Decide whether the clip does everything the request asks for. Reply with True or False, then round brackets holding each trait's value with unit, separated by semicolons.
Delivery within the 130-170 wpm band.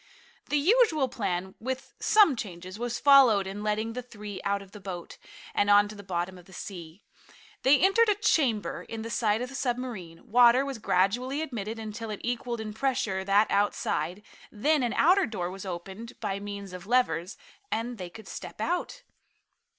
False (180 wpm)